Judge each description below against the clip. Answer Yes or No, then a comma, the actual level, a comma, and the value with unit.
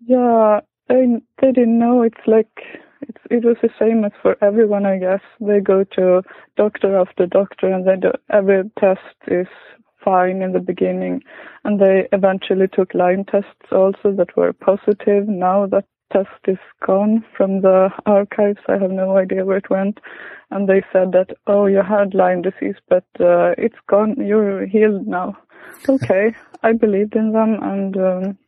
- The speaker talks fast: No, average, 170 wpm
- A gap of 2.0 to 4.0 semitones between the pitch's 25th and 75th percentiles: Yes, narrow, 2.4 semitones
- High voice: Yes, high, 200 Hz